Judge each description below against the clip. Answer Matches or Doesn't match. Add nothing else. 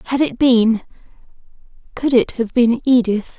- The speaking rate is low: Matches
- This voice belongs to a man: Doesn't match